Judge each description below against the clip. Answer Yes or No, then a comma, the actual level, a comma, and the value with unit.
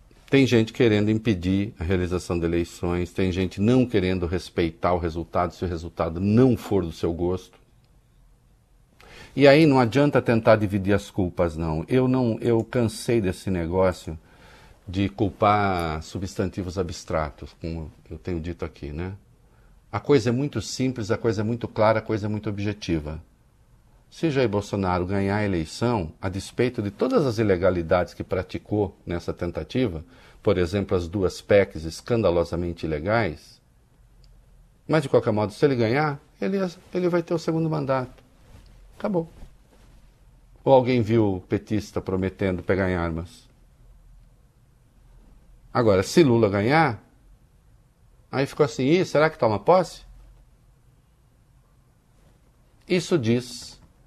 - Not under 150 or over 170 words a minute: No, average, 135 wpm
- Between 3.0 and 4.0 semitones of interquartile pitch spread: No, wide, 5.5 semitones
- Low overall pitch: Yes, low, 105 Hz